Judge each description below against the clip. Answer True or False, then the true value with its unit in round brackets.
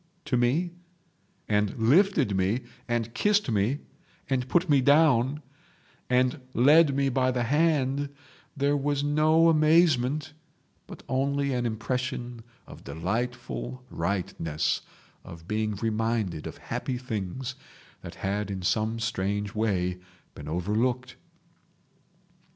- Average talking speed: False (115 wpm)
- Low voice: True (125 Hz)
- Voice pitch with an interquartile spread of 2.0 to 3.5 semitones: False (5.0 semitones)